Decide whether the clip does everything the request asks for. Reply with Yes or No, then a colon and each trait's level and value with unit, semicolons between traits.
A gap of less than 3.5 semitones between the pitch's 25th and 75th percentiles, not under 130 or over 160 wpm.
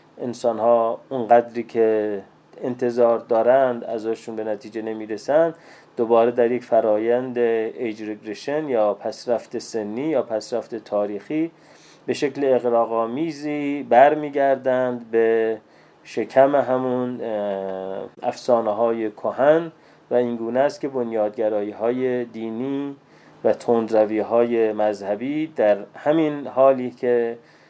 No: average, 3.1 semitones; average, 110 wpm